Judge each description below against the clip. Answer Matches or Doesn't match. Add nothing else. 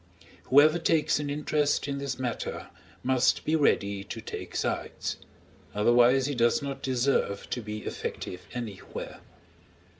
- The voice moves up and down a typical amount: Matches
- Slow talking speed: Matches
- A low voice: Matches